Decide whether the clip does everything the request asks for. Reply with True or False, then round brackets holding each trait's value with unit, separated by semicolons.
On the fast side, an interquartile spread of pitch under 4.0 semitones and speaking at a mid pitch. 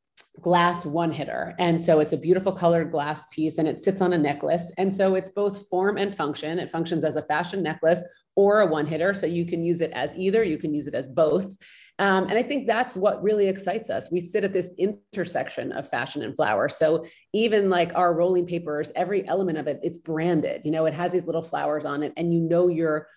True (235 wpm; 3.1 semitones; 175 Hz)